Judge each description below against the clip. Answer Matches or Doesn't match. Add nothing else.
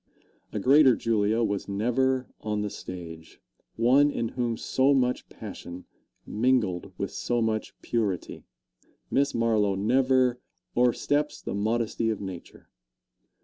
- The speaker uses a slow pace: Matches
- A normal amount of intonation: Matches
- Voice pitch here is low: Matches